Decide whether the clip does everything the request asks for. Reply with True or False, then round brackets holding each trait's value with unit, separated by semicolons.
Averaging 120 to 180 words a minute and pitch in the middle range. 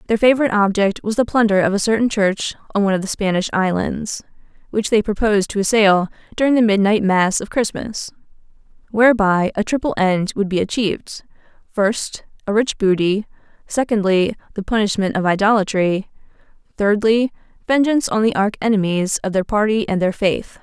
False (160 wpm; 205 Hz)